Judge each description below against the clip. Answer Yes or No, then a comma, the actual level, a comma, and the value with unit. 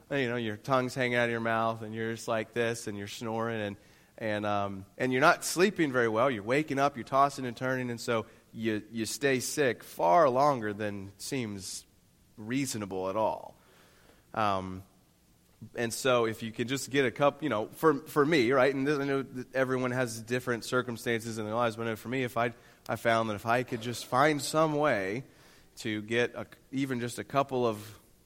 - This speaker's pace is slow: No, fast, 205 wpm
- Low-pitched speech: Yes, low, 120 Hz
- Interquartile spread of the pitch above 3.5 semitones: No, average, 2.9 semitones